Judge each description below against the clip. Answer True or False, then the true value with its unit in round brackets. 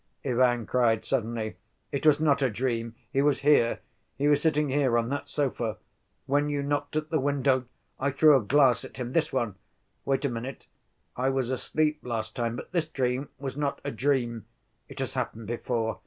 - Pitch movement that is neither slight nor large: True (3.4 semitones)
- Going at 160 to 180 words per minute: False (190 wpm)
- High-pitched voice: False (130 Hz)